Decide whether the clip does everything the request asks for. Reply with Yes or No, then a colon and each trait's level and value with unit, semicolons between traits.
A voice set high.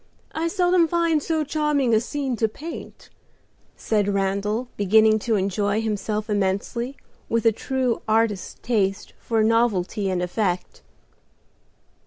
Yes: high, 220 Hz